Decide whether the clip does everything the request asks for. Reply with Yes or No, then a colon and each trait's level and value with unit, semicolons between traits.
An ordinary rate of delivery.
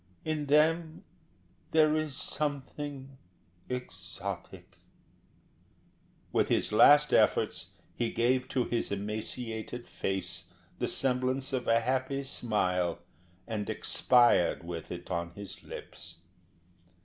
No: slow, 100 wpm